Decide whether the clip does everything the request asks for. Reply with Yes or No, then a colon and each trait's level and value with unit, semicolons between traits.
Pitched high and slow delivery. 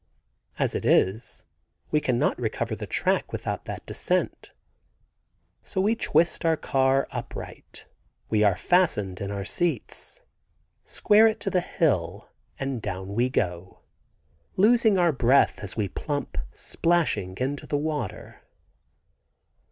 No: low, 135 Hz; slow, 130 wpm